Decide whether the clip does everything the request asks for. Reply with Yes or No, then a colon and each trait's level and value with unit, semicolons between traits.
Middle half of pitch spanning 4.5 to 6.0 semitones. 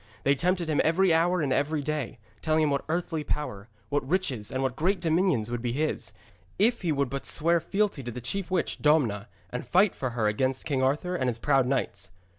Yes: average, 5.0 semitones